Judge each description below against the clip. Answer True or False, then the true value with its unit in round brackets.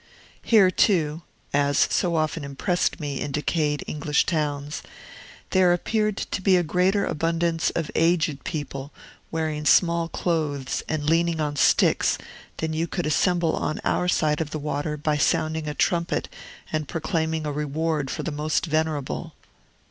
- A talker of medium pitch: True (160 Hz)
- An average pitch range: False (2.2 semitones)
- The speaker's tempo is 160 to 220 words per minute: False (150 wpm)